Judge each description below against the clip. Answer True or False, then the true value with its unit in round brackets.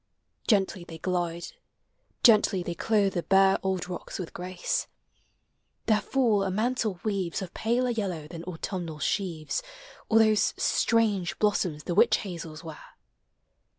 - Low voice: False (190 Hz)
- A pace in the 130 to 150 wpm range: True (135 wpm)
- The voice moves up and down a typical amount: True (3.7 semitones)